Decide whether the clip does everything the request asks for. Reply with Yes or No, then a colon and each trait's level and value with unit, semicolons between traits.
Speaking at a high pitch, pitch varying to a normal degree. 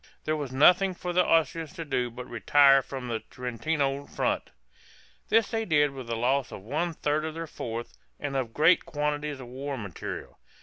No: medium, 140 Hz; average, 4.0 semitones